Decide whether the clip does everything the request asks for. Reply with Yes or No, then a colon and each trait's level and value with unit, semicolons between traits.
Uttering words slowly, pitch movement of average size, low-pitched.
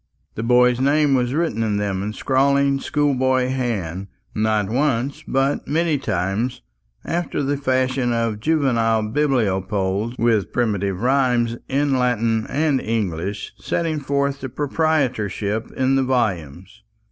Yes: slow, 130 wpm; average, 4.4 semitones; low, 125 Hz